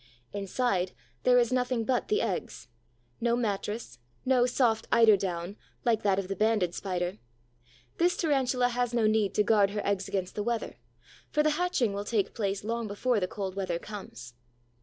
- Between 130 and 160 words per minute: No, average, 175 wpm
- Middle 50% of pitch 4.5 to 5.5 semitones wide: No, average, 3.8 semitones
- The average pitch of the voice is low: No, high, 215 Hz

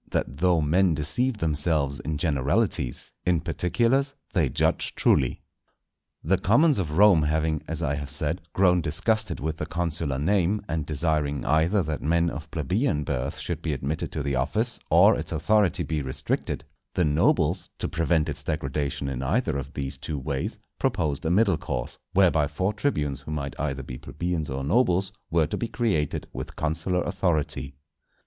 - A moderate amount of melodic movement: Yes, average, 3.8 semitones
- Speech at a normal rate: Yes, average, 170 wpm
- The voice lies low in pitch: Yes, very low, 80 Hz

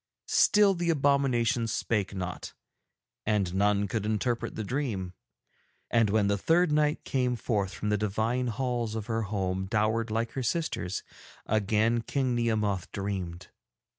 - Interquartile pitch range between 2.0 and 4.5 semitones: Yes, average, 3.6 semitones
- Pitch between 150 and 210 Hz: No, low, 110 Hz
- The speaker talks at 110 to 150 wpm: Yes, average, 140 wpm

